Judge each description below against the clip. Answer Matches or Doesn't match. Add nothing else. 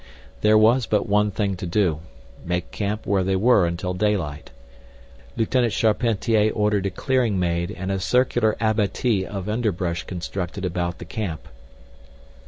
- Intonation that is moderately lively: Matches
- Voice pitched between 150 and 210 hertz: Doesn't match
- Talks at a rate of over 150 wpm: Doesn't match